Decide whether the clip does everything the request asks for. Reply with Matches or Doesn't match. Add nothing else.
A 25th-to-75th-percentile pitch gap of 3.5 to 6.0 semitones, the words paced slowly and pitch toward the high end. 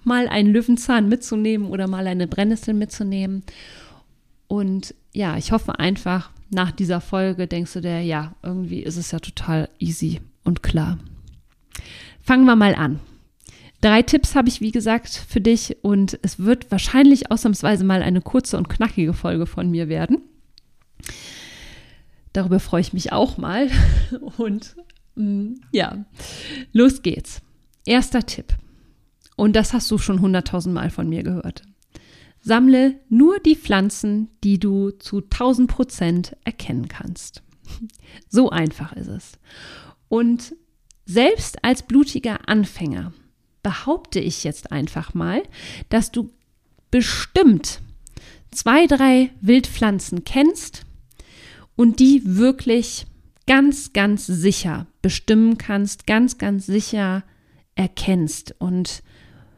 Matches